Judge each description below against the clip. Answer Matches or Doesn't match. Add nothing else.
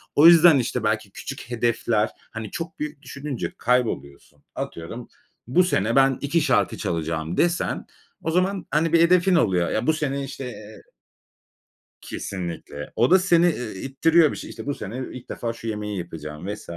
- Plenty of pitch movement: Matches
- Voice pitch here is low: Matches